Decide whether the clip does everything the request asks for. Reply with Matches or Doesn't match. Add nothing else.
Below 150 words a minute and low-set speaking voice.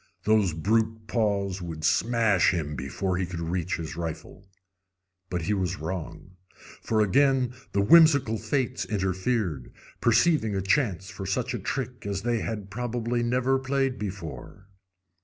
Matches